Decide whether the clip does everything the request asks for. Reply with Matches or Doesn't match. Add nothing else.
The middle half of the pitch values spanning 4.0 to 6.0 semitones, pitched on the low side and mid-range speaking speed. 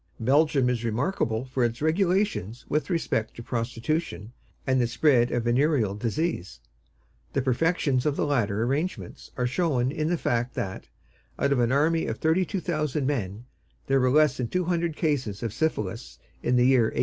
Matches